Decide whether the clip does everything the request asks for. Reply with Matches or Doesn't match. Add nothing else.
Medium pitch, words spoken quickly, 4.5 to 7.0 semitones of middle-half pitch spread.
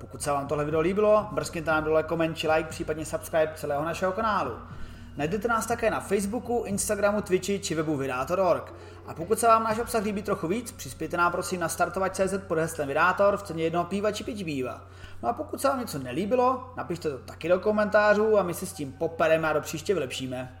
Matches